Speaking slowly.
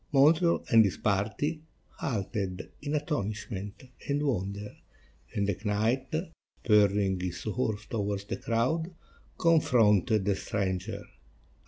Yes: slow, 110 wpm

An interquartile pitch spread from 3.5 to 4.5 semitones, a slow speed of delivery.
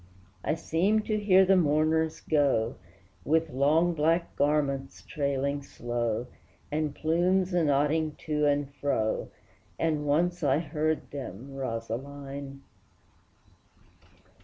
No: average, 2.7 semitones; slow, 105 wpm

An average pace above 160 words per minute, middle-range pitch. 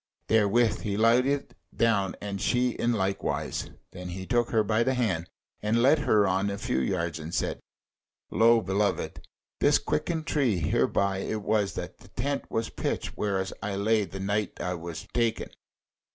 No: average, 170 wpm; low, 105 Hz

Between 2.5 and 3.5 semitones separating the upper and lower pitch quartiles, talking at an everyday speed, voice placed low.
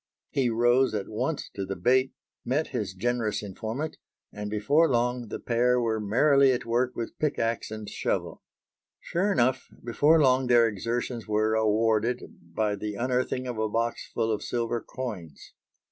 Yes: average, 2.8 semitones; average, 160 wpm; low, 115 Hz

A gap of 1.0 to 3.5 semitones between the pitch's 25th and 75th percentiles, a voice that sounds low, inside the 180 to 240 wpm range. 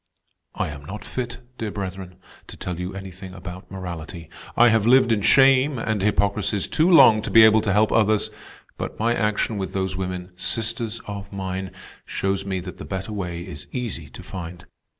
Yes: average, 3.2 semitones; low, 100 Hz; average, 185 wpm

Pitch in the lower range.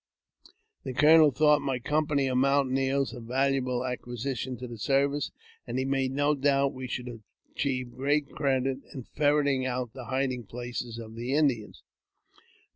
Yes: low, 130 Hz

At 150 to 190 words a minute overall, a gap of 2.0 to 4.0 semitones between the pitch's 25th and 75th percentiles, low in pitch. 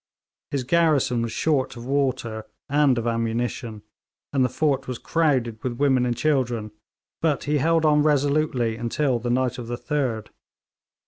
Yes: average, 155 wpm; average, 3.7 semitones; low, 130 Hz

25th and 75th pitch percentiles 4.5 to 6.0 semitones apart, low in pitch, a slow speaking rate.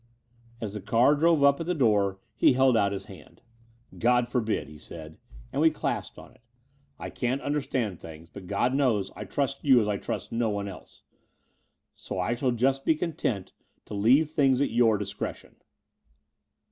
No: wide, 5.4 semitones; low, 120 Hz; average, 180 wpm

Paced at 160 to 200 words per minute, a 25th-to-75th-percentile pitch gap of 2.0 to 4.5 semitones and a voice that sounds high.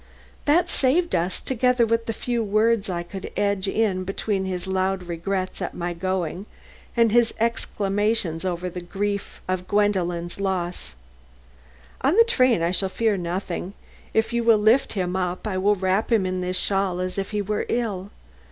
Yes: average, 170 wpm; average, 3.3 semitones; high, 195 Hz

